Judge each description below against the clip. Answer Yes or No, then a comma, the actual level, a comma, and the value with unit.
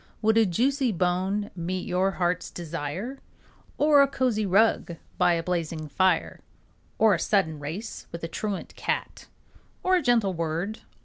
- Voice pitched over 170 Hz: Yes, high, 190 Hz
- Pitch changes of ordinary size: Yes, average, 4.7 semitones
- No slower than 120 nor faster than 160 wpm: Yes, average, 150 wpm